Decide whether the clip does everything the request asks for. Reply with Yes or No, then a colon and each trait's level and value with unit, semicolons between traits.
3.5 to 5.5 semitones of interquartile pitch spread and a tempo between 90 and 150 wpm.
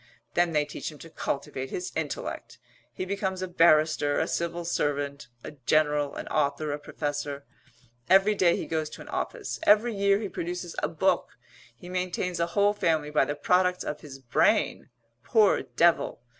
No: average, 4.0 semitones; average, 170 wpm